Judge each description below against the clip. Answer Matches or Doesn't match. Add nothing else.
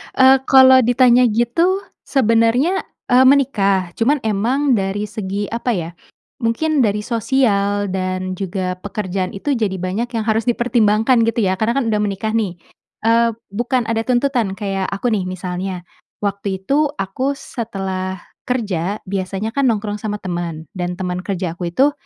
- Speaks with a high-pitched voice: Matches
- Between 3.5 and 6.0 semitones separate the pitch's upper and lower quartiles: Matches